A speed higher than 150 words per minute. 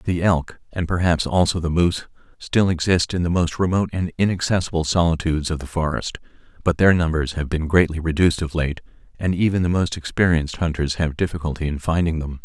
Yes: average, 190 wpm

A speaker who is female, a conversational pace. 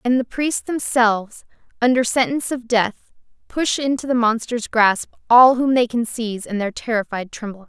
Yes: female; average, 180 wpm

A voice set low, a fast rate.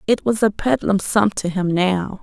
No: high, 200 Hz; fast, 215 wpm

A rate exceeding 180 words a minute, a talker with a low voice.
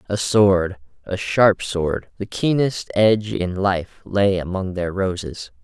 No: average, 150 wpm; very low, 95 Hz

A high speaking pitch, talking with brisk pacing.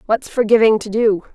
No: high, 220 Hz; average, 180 wpm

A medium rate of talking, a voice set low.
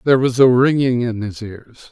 No: fast, 220 wpm; low, 120 Hz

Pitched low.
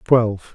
Yes: low, 110 Hz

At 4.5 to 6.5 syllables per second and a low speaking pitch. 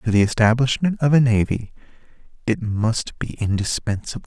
Yes: 5.1 syllables/s; low, 115 Hz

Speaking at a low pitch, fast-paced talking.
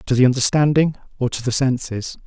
No: low, 130 Hz; average, 185 wpm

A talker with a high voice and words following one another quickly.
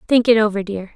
Yes: high, 215 Hz; fast, 250 wpm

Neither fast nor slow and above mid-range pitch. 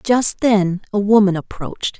Yes: average, 150 wpm; high, 205 Hz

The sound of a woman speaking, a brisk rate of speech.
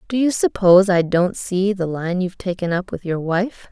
Yes: female; fast, 225 wpm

